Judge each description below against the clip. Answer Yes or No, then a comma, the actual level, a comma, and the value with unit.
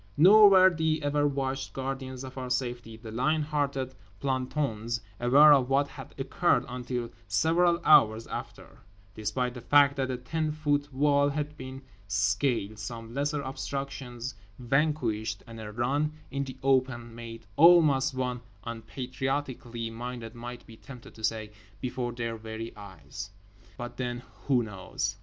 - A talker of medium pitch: No, low, 130 Hz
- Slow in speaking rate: No, average, 145 wpm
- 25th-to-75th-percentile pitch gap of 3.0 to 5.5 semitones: Yes, average, 3.6 semitones